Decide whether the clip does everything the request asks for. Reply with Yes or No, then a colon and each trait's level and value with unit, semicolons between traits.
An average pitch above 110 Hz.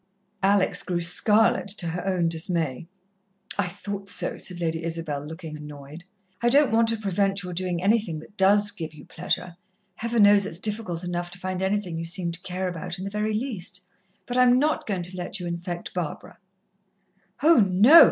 Yes: medium, 185 Hz